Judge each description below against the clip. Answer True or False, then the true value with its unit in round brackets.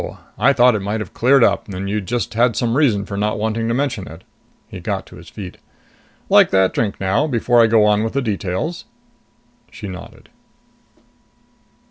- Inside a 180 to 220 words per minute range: True (185 wpm)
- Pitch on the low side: True (110 Hz)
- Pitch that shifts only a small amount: False (3.4 semitones)